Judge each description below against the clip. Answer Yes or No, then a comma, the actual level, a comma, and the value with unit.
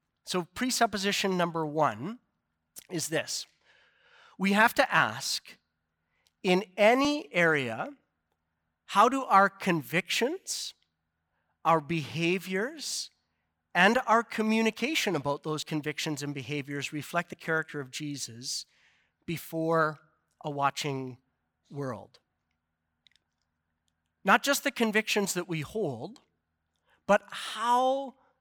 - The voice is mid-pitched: Yes, medium, 160 Hz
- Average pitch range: No, wide, 7.4 semitones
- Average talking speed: No, slow, 95 wpm